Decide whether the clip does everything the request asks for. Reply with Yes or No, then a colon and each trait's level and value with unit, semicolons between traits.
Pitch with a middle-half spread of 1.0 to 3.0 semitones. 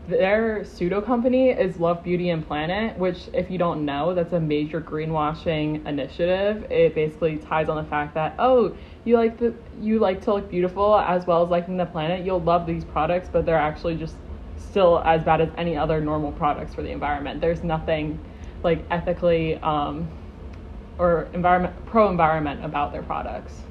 Yes: average, 2.7 semitones